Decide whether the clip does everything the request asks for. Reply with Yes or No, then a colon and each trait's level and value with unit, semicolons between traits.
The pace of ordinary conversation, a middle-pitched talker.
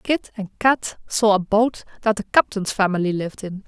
No: average, 195 wpm; high, 205 Hz